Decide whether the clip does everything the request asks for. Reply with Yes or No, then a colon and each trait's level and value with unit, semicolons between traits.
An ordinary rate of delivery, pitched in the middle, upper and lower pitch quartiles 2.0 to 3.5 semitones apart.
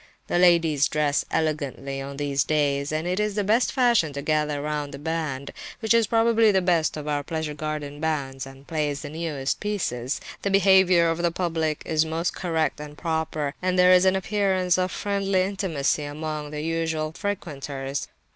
No: average, 175 wpm; medium, 160 Hz; average, 3.9 semitones